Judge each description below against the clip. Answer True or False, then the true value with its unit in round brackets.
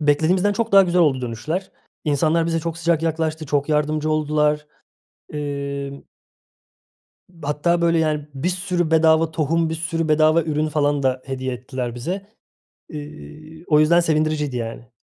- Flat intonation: True (2.2 semitones)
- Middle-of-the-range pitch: True (155 Hz)